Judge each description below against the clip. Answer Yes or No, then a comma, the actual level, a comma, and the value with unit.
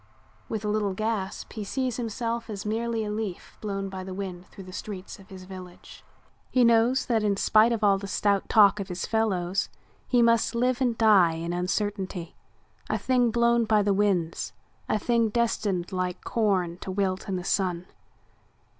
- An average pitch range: Yes, average, 3.3 semitones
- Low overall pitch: No, high, 205 Hz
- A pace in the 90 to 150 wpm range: No, average, 180 wpm